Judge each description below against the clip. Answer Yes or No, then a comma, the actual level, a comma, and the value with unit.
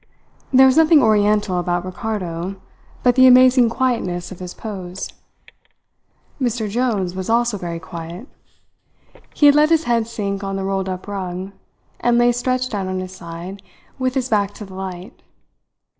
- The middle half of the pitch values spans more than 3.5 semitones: Yes, average, 4.8 semitones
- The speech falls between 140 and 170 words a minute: Yes, average, 160 wpm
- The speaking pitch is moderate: No, high, 205 Hz